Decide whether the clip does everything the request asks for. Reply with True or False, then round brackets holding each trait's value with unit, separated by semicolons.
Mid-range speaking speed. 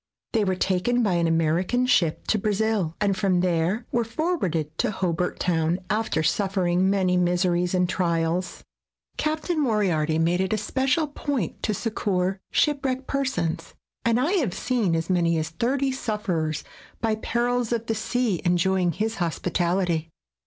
True (150 wpm)